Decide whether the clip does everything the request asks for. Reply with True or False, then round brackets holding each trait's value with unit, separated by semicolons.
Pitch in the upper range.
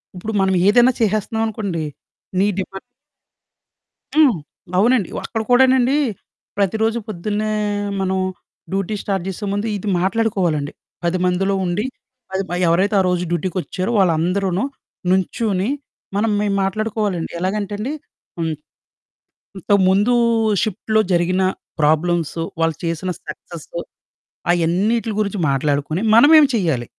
True (195 Hz)